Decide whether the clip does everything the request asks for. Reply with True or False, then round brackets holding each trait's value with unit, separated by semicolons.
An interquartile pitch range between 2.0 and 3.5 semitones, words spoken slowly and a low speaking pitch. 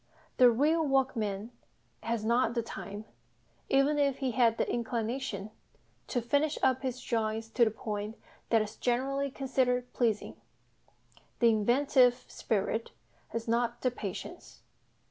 False (2.9 semitones; 130 wpm; 240 Hz)